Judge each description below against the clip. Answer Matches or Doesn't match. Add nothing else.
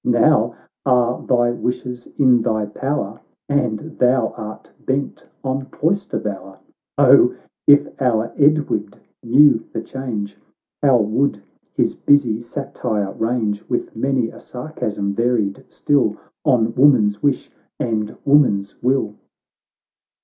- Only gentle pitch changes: Doesn't match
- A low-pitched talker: Matches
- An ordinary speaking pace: Doesn't match